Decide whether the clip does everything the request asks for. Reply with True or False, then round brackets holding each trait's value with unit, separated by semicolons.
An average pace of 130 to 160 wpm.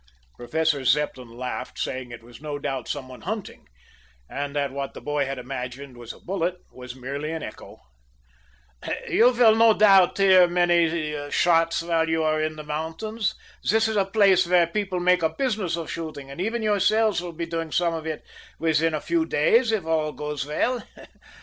False (185 wpm)